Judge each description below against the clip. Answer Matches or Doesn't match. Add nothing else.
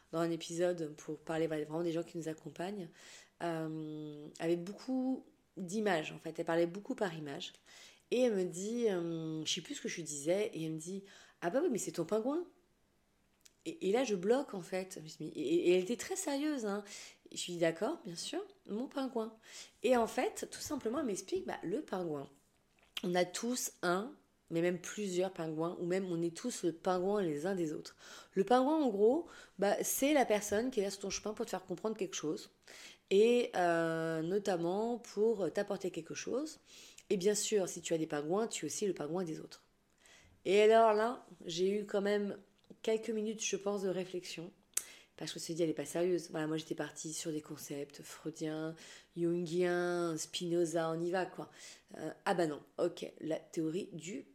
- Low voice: Doesn't match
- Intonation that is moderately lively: Matches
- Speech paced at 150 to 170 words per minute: Doesn't match